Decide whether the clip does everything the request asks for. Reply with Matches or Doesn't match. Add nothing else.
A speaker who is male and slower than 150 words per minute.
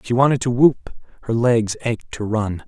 Doesn't match